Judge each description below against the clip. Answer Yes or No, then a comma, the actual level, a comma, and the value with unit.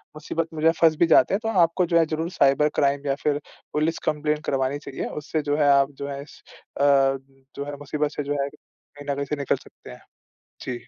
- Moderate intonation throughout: No, narrow, 1.9 semitones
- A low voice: No, medium, 145 Hz